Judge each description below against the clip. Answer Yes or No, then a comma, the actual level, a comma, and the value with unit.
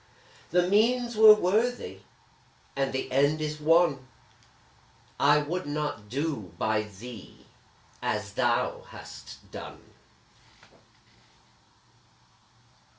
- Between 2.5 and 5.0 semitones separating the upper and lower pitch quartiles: No, wide, 5.5 semitones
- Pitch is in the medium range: Yes, medium, 150 Hz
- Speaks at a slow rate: Yes, slow, 90 wpm